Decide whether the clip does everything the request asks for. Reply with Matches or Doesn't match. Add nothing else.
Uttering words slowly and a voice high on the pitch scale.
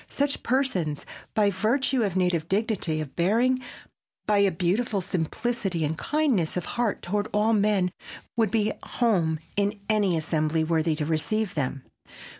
Doesn't match